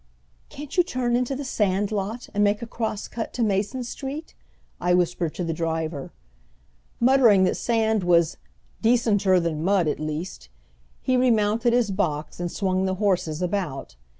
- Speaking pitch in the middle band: No, high, 200 Hz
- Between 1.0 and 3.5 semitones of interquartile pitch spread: No, average, 5.0 semitones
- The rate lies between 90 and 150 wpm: No, average, 160 wpm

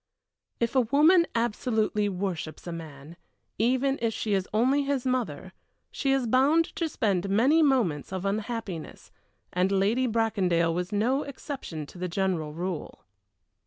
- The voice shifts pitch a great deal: Yes, wide, 6.1 semitones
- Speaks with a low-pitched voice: No, high, 215 Hz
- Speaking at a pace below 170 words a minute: Yes, average, 145 wpm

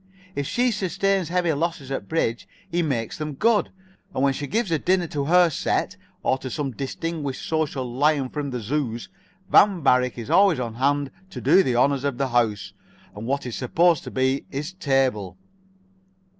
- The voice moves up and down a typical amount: Yes, average, 4.7 semitones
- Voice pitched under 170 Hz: Yes, medium, 140 Hz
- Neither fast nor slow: Yes, average, 185 wpm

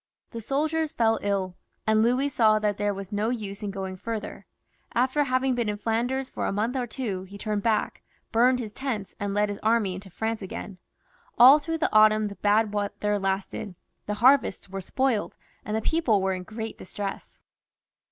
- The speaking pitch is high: Yes, high, 215 Hz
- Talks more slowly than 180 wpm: No, average, 190 wpm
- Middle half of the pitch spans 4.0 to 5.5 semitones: No, average, 3.3 semitones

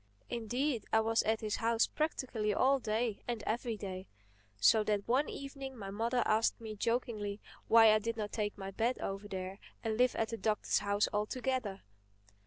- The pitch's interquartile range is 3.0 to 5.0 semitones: No, narrow, 2.6 semitones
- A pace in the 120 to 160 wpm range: No, average, 180 wpm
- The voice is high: Yes, high, 220 Hz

